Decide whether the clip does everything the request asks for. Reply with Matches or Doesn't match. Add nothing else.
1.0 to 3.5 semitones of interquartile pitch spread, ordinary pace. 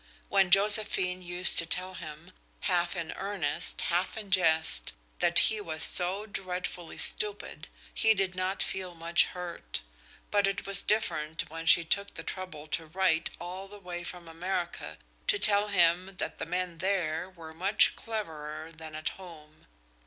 Matches